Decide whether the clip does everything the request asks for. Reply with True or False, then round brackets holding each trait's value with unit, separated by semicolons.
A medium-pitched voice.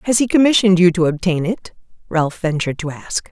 True (180 Hz)